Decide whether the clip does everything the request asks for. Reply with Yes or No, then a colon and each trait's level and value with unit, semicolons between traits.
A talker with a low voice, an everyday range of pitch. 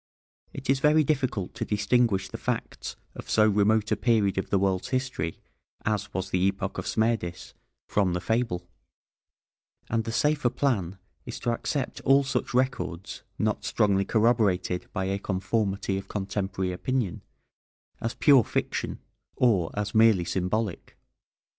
Yes: low, 105 Hz; average, 3.9 semitones